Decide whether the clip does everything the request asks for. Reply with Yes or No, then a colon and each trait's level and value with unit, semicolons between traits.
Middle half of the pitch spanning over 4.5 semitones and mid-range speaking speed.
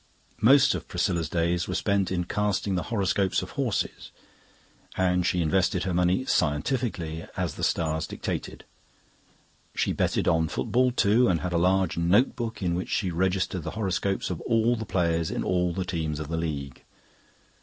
No: average, 3.2 semitones; average, 165 wpm